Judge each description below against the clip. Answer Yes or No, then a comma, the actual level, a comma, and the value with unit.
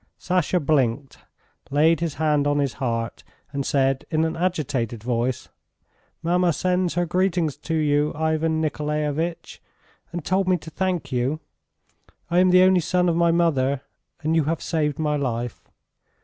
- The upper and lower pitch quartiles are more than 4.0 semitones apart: No, average, 3.5 semitones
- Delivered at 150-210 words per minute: Yes, average, 155 wpm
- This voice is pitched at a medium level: Yes, medium, 155 Hz